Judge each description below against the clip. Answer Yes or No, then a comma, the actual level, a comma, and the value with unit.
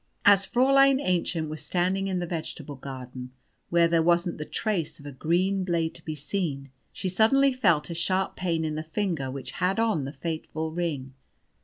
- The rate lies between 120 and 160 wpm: No, average, 185 wpm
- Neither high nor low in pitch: Yes, medium, 170 Hz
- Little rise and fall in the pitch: No, average, 3.8 semitones